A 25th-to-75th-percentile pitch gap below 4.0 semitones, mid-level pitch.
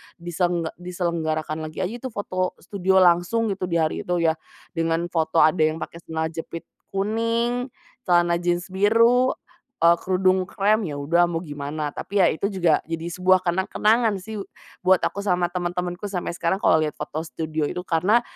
Yes: average, 3.0 semitones; medium, 175 Hz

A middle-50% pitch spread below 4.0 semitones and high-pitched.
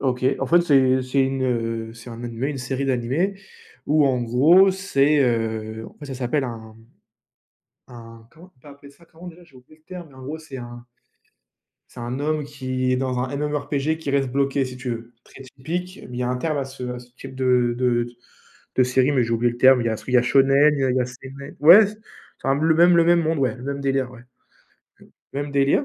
No: average, 3.0 semitones; low, 135 Hz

